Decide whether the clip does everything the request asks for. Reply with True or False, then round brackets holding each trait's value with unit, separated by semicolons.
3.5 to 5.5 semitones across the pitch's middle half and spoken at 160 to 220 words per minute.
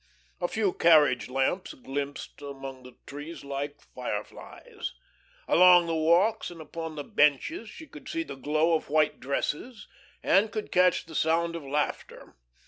False (4.1 semitones; 150 wpm)